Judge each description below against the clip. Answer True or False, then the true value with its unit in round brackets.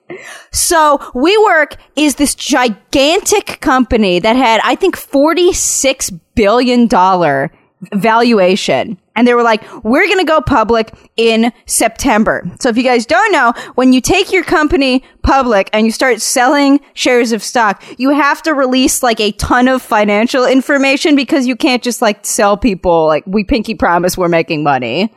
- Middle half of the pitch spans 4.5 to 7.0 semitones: True (4.9 semitones)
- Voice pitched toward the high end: True (250 Hz)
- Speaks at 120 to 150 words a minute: False (160 wpm)